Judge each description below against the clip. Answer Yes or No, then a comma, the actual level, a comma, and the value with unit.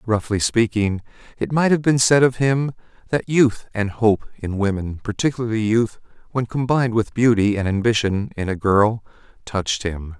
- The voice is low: Yes, low, 110 Hz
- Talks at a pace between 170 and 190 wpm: No, average, 155 wpm